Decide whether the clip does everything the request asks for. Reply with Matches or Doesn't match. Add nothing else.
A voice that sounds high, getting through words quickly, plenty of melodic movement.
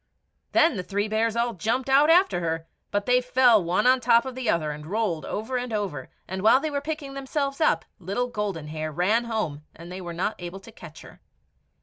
Matches